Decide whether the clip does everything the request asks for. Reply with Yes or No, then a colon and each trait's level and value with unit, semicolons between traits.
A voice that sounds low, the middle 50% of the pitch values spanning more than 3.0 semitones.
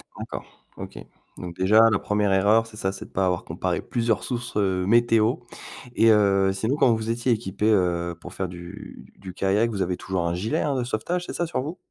Yes: low, 105 Hz; average, 3.4 semitones